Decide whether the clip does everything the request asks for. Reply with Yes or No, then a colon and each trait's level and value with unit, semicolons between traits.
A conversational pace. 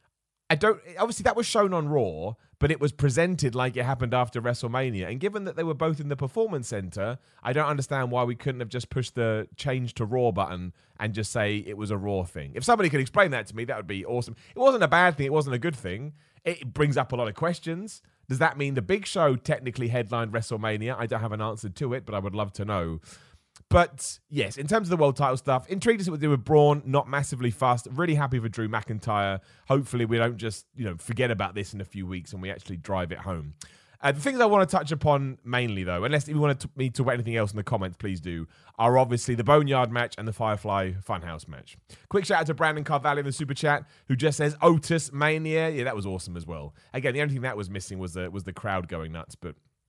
No: fast, 255 wpm